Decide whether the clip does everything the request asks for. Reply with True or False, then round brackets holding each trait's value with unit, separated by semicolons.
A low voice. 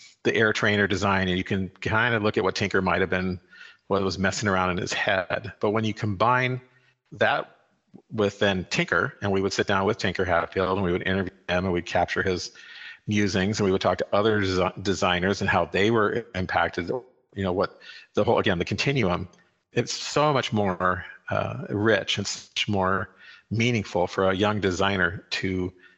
True (95 Hz)